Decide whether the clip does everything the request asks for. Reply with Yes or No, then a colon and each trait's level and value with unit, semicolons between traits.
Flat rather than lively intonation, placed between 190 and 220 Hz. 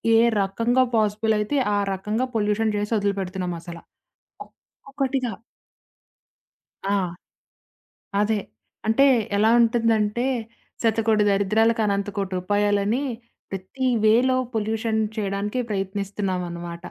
Yes: narrow, 2.3 semitones; high, 210 Hz